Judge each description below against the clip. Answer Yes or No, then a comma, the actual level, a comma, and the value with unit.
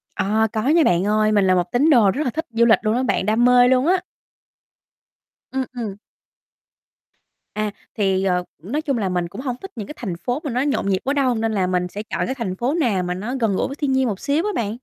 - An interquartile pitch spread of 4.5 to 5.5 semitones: Yes, average, 5.1 semitones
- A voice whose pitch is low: No, high, 230 Hz